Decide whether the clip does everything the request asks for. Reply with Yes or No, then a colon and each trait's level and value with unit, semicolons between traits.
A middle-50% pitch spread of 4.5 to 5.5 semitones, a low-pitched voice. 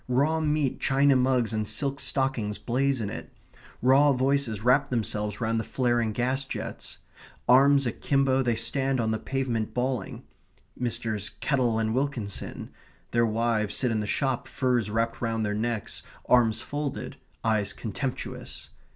No: average, 3.3 semitones; low, 125 Hz